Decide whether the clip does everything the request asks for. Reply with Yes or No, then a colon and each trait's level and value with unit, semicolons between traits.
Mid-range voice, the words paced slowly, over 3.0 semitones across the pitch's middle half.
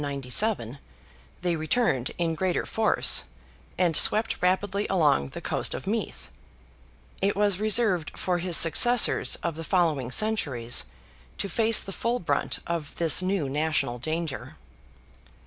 Yes: medium, 170 Hz; slow, 130 wpm; average, 5.2 semitones